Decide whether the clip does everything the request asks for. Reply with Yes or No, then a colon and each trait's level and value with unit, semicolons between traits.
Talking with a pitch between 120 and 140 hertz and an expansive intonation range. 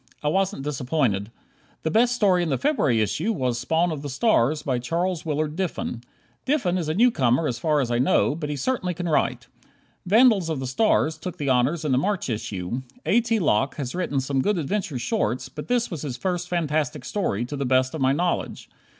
No: medium, 150 Hz; wide, 5.7 semitones